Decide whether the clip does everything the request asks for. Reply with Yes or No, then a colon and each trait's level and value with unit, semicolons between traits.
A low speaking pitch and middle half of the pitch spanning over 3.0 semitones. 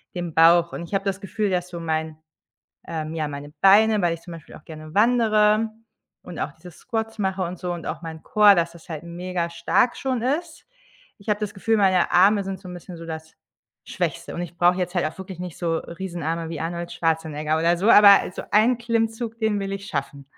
No: medium, 180 Hz; average, 3.8 semitones